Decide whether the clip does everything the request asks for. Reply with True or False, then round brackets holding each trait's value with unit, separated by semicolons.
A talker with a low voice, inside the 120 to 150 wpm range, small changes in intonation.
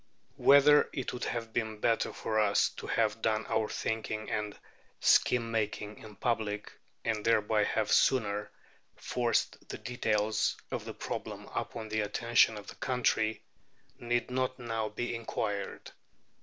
True (110 Hz; 140 wpm; 1.9 semitones)